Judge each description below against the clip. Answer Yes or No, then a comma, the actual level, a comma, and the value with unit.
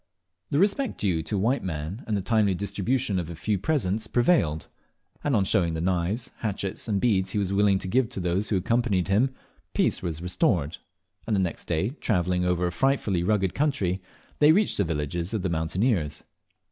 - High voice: No, very low, 95 Hz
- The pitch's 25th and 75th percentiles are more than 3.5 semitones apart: Yes, average, 4.4 semitones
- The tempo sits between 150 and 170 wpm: No, average, 195 wpm